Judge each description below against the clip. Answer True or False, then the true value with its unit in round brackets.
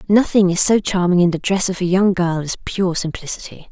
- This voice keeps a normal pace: False (225 wpm)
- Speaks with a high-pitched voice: False (180 Hz)